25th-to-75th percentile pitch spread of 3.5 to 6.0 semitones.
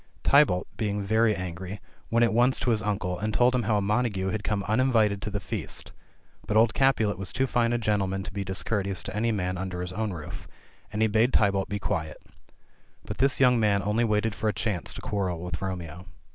No: average, 2.9 semitones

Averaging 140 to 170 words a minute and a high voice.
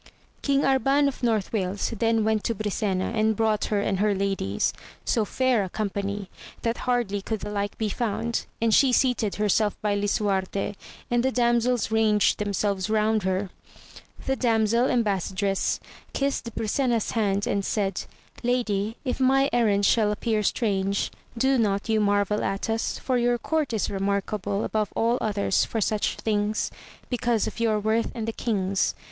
Yes: average, 165 wpm; high, 215 Hz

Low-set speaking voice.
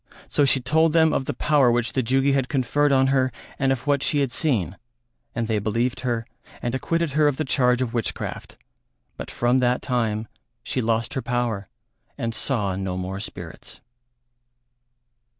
Yes: low, 125 Hz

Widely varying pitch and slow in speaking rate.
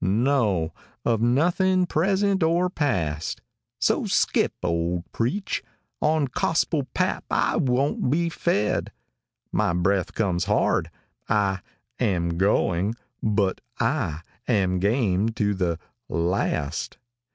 Yes: wide, 8.2 semitones; slow, 105 wpm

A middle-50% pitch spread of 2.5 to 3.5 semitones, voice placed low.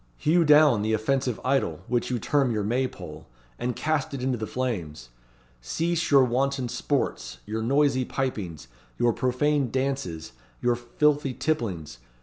No: average, 4.0 semitones; low, 125 Hz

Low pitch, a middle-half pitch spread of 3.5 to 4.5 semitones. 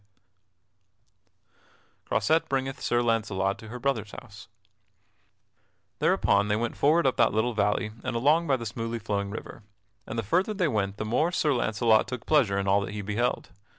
Yes: low, 110 Hz; average, 3.9 semitones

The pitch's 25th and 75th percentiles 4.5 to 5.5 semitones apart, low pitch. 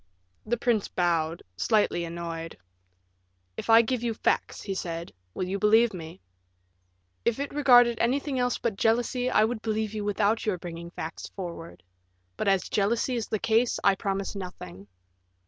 No: average, 5.0 semitones; high, 210 Hz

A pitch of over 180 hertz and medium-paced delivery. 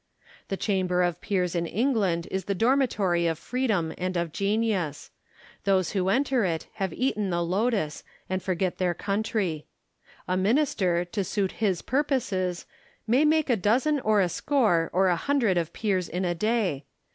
Yes: high, 190 Hz; average, 165 wpm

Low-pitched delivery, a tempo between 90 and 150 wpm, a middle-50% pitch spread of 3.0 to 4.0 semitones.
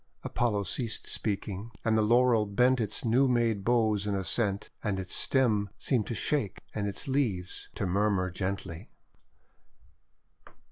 Yes: low, 105 Hz; average, 140 wpm; average, 3.3 semitones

